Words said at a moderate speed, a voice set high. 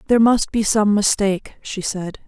Yes: average, 185 wpm; high, 205 Hz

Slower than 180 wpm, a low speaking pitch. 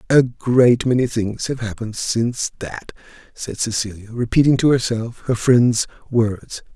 Yes: average, 140 wpm; low, 120 Hz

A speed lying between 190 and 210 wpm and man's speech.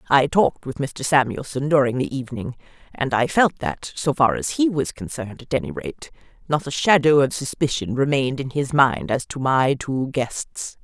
No: average, 195 wpm; female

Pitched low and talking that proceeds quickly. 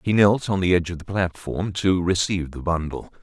Yes: very low, 90 Hz; fast, 225 wpm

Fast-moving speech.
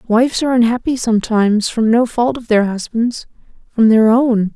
No: average, 160 wpm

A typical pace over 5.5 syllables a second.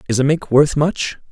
No: 5.0 syllables/s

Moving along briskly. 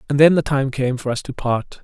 Yes: fast, 295 wpm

